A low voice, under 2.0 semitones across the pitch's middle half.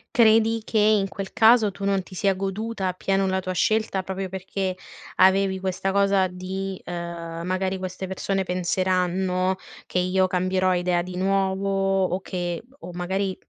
No: high, 190 Hz; narrow, 1.1 semitones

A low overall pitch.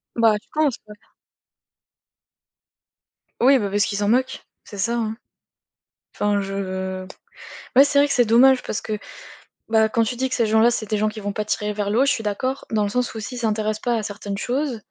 No: high, 220 Hz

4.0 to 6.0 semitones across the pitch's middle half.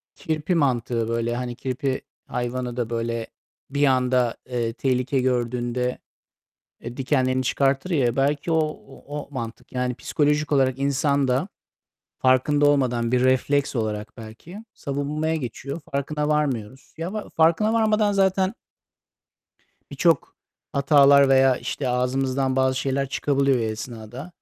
No: average, 2.9 semitones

